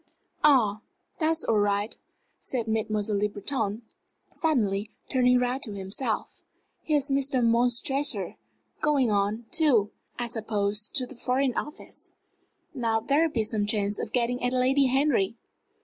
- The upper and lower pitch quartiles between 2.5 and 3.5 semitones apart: No, average, 4.3 semitones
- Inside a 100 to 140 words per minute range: Yes, slow, 135 wpm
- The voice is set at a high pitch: Yes, high, 235 Hz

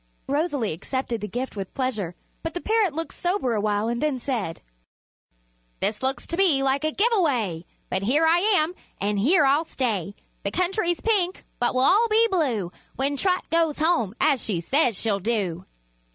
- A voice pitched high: Yes, very high, 270 Hz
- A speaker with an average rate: Yes, average, 180 wpm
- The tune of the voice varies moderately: No, wide, 8.0 semitones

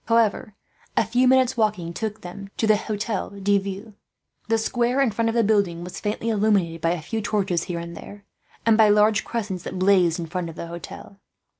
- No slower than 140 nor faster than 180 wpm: No, fast, 205 wpm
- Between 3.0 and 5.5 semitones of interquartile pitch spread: Yes, average, 3.6 semitones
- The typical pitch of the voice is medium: No, high, 205 Hz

